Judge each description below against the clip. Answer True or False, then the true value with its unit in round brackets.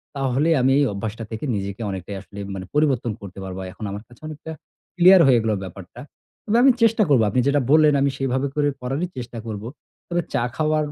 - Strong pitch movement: True (6.6 semitones)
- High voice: False (130 Hz)